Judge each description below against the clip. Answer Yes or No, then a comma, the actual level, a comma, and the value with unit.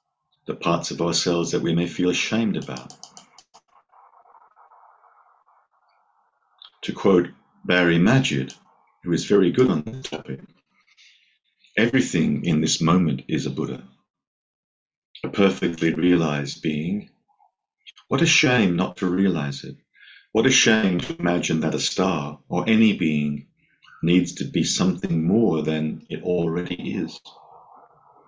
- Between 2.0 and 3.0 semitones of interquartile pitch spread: Yes, narrow, 2.6 semitones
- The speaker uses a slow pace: Yes, slow, 125 wpm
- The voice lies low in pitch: Yes, very low, 85 Hz